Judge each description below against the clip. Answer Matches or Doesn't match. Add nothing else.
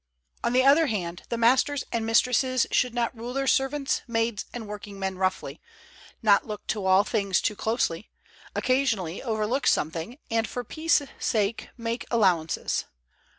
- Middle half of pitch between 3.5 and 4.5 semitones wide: Matches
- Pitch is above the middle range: Matches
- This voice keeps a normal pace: Matches